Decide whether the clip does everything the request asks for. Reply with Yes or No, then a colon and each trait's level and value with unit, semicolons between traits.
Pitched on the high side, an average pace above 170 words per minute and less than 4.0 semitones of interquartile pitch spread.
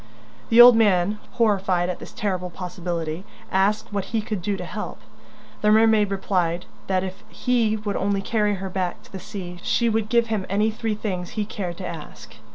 Yes: high, 200 Hz; average, 190 wpm; average, 3.0 semitones